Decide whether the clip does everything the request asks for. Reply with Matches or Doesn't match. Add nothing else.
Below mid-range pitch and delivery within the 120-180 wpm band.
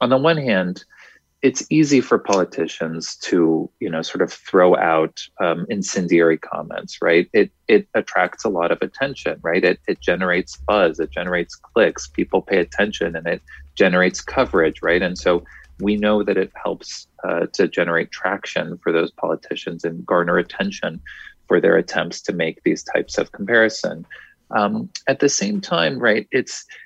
Matches